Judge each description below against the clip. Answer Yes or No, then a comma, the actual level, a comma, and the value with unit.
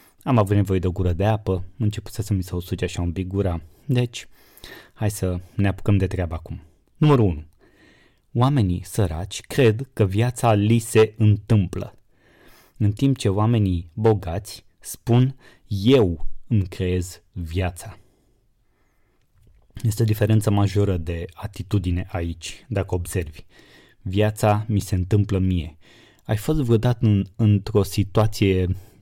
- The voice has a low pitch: Yes, low, 100 Hz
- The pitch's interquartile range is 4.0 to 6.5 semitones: No, average, 3.3 semitones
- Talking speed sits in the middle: Yes, average, 140 wpm